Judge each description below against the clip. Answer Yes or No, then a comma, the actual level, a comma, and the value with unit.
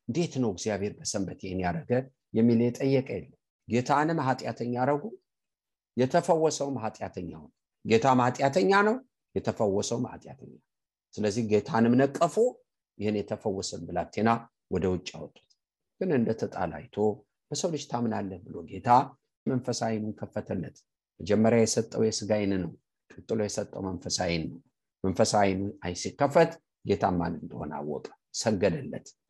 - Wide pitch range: No, average, 5.0 semitones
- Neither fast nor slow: No, slow, 105 wpm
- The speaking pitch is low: Yes, low, 115 Hz